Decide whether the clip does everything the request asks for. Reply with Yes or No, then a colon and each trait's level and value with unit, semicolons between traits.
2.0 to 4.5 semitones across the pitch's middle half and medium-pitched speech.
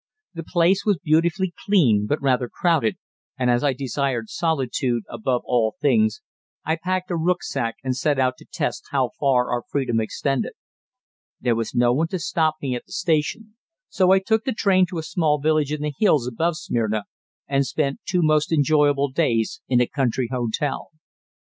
No: average, 5.3 semitones; medium, 145 Hz